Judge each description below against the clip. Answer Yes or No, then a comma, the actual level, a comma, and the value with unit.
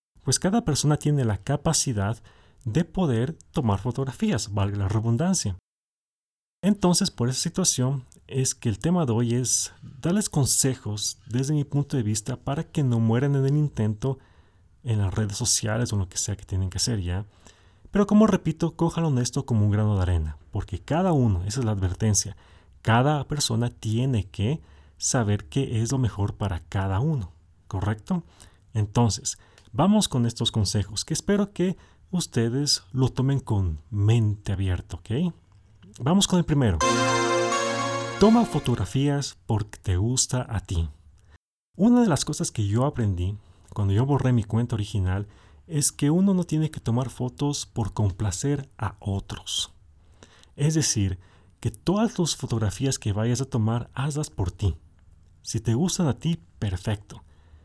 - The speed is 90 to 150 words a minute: No, average, 160 wpm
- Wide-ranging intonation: Yes, wide, 6.2 semitones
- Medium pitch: No, low, 115 Hz